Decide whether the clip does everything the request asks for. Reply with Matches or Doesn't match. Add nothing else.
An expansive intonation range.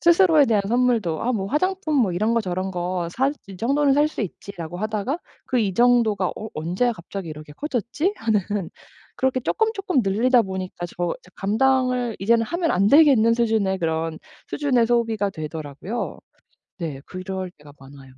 Matches